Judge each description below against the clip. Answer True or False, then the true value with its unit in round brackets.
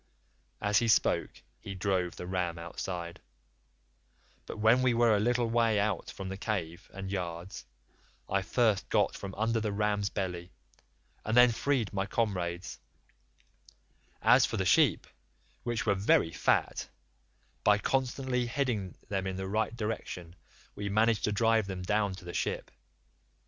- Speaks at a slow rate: False (150 wpm)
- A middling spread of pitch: True (3.3 semitones)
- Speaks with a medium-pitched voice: False (100 Hz)